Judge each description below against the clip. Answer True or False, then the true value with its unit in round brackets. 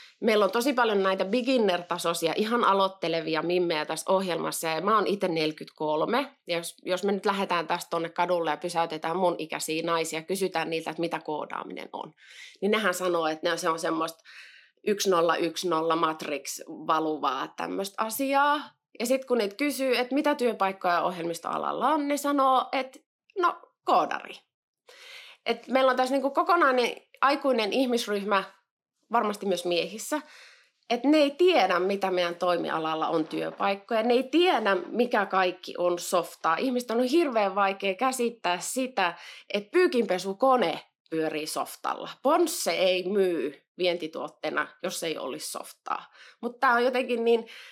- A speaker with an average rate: True (140 wpm)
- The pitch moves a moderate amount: False (6.9 semitones)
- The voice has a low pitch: False (195 Hz)